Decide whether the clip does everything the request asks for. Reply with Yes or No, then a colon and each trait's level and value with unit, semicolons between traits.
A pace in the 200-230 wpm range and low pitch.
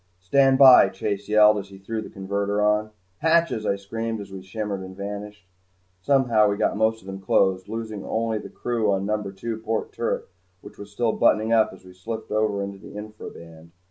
Yes: fast, 205 wpm; low, 105 Hz